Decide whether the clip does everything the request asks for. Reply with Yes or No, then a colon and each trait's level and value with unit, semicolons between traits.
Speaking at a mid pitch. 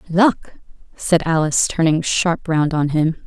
Yes: medium, 165 Hz